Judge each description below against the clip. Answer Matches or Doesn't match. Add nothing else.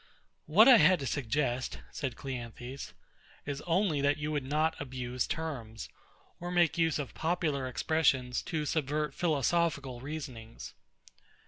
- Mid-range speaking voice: Matches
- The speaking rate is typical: Doesn't match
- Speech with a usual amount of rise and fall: Matches